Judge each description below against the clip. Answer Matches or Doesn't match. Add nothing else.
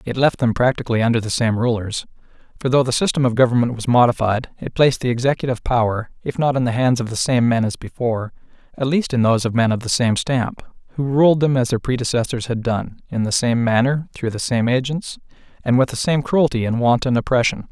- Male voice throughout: Matches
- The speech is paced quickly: Matches